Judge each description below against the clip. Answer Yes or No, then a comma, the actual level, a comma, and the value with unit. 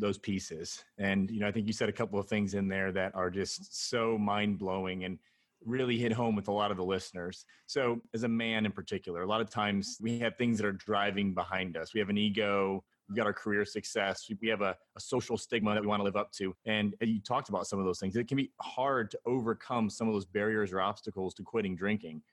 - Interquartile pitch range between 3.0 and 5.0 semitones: No, narrow, 2.4 semitones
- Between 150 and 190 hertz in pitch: No, low, 105 Hz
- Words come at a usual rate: No, fast, 255 wpm